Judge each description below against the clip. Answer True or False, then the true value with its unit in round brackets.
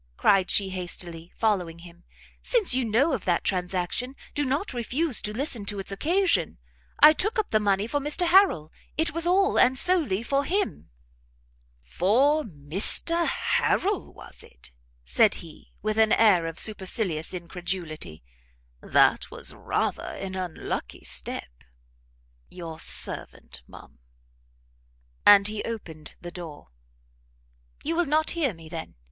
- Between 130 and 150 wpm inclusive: True (140 wpm)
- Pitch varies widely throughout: True (8.9 semitones)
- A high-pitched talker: True (210 Hz)